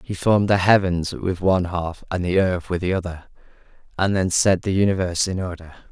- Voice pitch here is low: Yes, very low, 90 Hz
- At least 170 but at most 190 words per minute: No, fast, 205 wpm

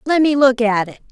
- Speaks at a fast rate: Yes, fast, 215 wpm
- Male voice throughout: No, female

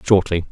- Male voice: Yes, male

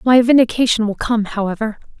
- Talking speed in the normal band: Yes, average, 150 wpm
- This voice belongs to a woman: Yes, female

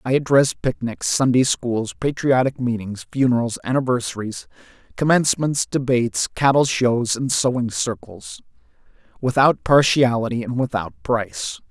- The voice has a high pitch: No, low, 125 Hz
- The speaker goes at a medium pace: No, slow, 110 wpm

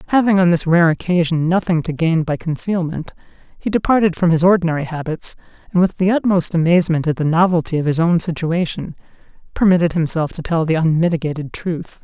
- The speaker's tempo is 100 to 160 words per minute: No, average, 175 wpm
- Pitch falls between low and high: Yes, medium, 170 Hz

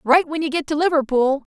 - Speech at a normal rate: No, fast, 230 wpm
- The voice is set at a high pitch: Yes, very high, 300 Hz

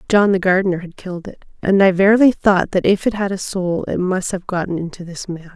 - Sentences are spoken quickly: Yes, fast, 250 wpm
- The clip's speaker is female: Yes, female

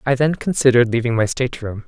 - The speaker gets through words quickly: No, average, 190 wpm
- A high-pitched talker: No, low, 125 Hz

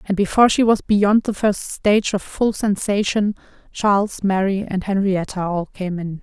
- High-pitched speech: Yes, high, 200 Hz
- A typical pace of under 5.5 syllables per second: Yes, 4.7 syllables/s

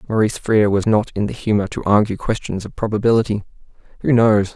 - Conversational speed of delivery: Yes, average, 185 wpm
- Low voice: Yes, low, 105 Hz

